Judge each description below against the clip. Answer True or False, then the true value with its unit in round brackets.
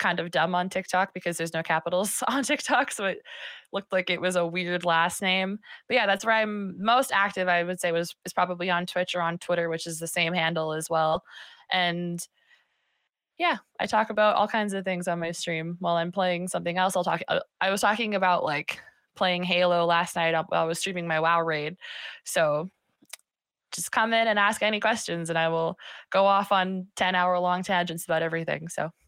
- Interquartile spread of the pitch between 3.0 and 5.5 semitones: False (2.6 semitones)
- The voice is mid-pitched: True (180 Hz)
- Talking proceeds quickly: True (210 wpm)